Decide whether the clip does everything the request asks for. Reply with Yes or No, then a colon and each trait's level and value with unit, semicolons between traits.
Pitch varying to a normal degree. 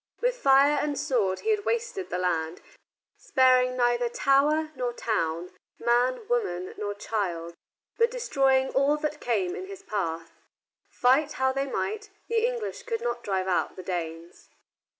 No: wide, 8.2 semitones